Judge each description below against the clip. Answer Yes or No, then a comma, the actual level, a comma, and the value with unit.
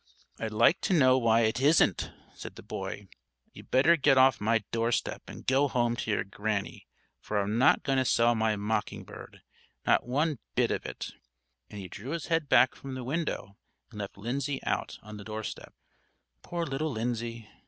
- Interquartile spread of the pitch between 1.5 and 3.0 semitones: No, average, 3.8 semitones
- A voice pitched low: Yes, low, 120 Hz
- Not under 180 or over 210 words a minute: Yes, average, 185 wpm